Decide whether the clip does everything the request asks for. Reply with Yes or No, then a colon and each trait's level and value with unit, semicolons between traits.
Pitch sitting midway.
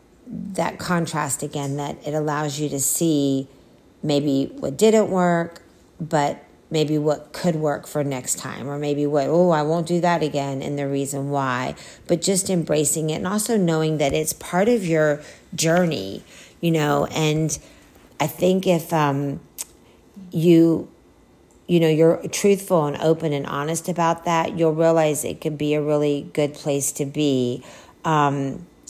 Yes: medium, 155 Hz